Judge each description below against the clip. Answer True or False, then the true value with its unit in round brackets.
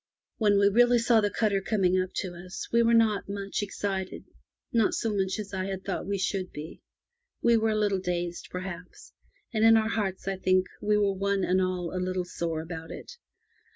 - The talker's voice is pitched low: False (195 Hz)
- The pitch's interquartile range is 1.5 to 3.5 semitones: True (2.6 semitones)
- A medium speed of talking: False (210 wpm)